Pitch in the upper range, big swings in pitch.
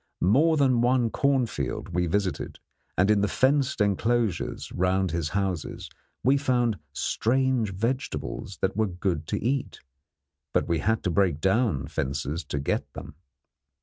No: low, 100 Hz; wide, 5.9 semitones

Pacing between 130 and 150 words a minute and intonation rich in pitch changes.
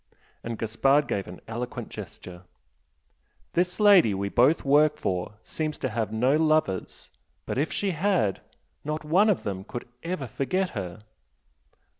Yes: average, 145 wpm; wide, 7.1 semitones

